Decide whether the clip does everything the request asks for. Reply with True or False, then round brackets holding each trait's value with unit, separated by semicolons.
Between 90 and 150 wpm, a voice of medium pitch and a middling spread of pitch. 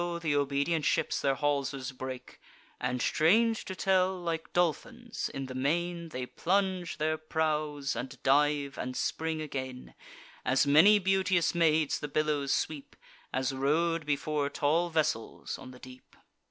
True (140 wpm; 155 Hz; 3.8 semitones)